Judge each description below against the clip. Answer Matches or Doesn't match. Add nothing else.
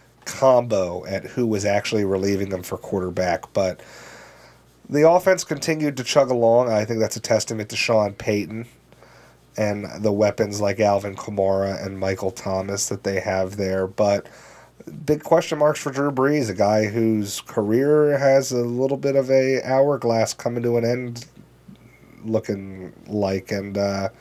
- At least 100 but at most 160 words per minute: Matches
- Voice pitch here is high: Doesn't match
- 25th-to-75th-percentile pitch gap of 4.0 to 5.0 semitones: Matches